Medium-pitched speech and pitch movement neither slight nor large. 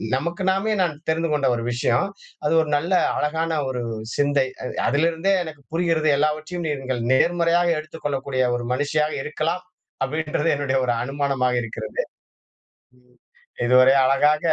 Yes: medium, 150 Hz; average, 3.5 semitones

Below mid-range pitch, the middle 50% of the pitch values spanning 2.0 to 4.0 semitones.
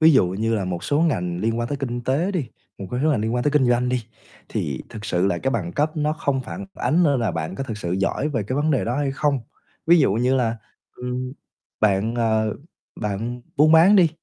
No: low, 125 Hz; average, 5.2 semitones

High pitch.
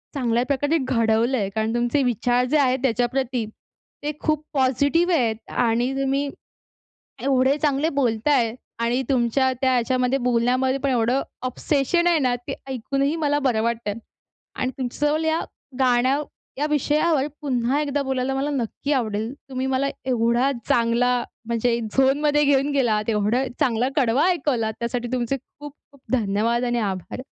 Yes: very high, 255 Hz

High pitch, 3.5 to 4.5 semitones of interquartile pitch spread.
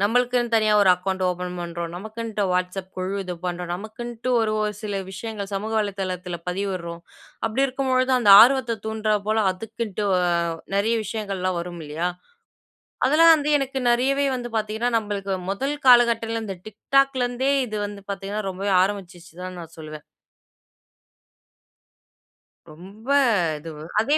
Yes: high, 210 Hz; average, 4.2 semitones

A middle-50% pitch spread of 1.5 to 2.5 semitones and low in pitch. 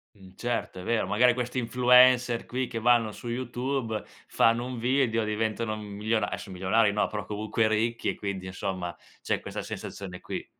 No: average, 2.9 semitones; low, 115 Hz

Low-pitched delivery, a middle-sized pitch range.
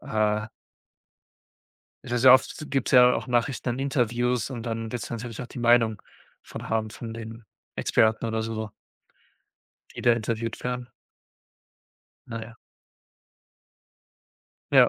No: low, 115 Hz; narrow, 1.8 semitones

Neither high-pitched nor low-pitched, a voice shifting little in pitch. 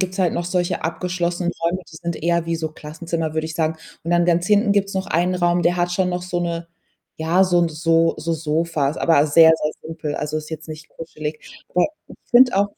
Yes: medium, 170 Hz; narrow, 1.9 semitones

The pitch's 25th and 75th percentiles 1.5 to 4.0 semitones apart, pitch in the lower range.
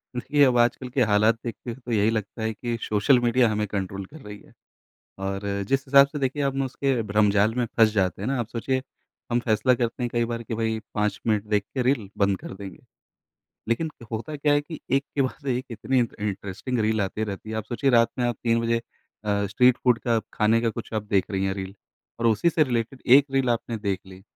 Yes: average, 3.5 semitones; low, 115 Hz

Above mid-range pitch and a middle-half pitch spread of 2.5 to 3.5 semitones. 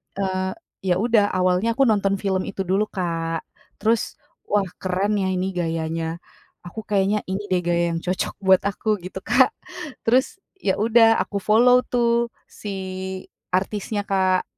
Yes: high, 195 Hz; average, 3.0 semitones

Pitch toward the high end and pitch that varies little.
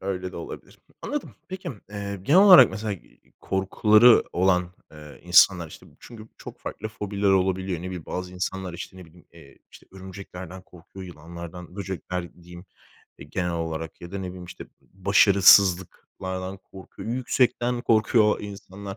No: very low, 95 Hz; narrow, 2.3 semitones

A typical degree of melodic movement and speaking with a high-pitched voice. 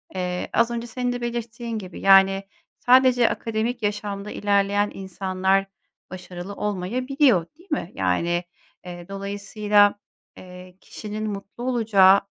Yes: average, 3.7 semitones; high, 205 Hz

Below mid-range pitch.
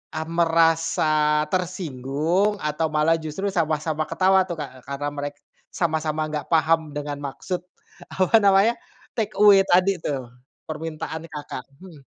No: medium, 160 Hz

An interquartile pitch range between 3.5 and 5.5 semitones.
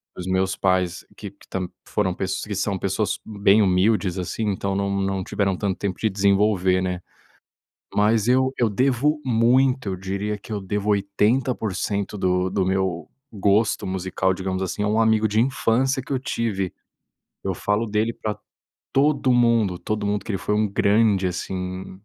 No: average, 2.8 semitones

